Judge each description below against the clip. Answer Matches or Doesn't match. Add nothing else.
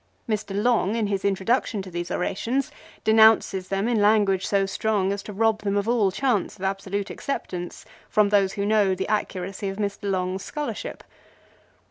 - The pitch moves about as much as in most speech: Doesn't match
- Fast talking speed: Doesn't match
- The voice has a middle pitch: Doesn't match